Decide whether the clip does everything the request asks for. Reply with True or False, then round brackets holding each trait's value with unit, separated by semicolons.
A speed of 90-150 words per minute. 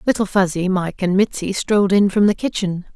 False (205 wpm)